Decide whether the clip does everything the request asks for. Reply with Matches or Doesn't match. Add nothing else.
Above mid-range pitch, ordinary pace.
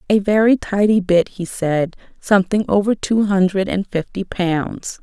Matches